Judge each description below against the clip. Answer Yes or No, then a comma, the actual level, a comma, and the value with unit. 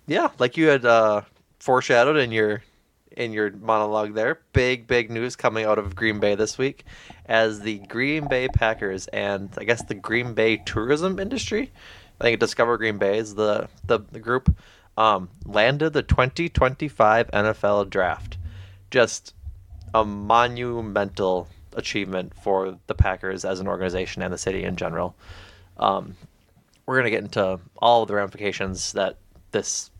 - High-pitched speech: No, low, 105 Hz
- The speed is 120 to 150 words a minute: No, average, 160 wpm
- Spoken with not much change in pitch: No, average, 3.5 semitones